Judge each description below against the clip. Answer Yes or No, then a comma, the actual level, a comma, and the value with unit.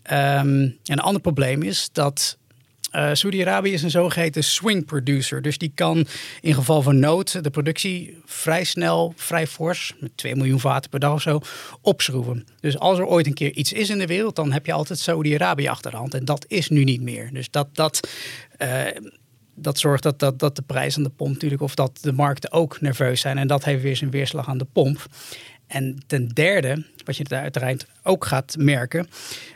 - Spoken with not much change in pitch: No, average, 3.1 semitones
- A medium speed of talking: No, fast, 205 wpm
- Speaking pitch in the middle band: Yes, medium, 145 Hz